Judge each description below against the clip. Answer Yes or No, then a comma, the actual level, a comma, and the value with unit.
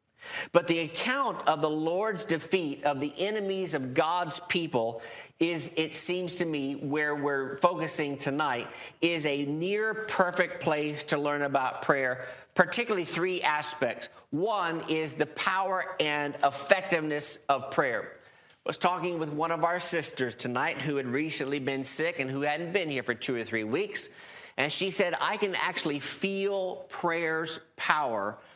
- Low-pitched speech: No, medium, 160 Hz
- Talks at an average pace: Yes, average, 160 wpm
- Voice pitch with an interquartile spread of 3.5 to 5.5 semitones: Yes, average, 4.0 semitones